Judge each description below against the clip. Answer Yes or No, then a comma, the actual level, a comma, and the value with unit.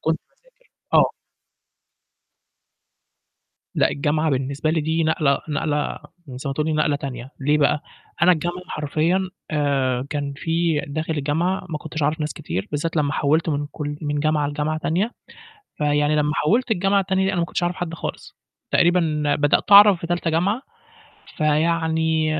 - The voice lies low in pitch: No, medium, 155 Hz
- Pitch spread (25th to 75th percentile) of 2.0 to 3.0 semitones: Yes, narrow, 2.5 semitones